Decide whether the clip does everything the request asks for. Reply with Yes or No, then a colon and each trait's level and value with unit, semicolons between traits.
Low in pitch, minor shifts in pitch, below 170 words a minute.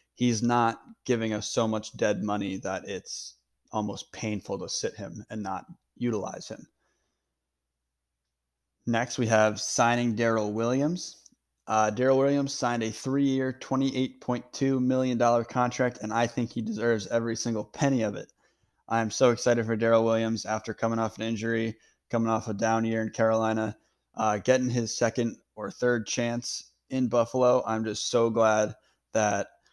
Yes: low, 115 Hz; narrow, 2.1 semitones; average, 155 wpm